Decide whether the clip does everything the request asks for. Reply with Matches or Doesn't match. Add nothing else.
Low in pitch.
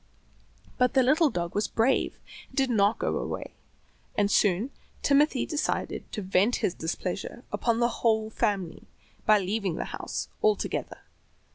Doesn't match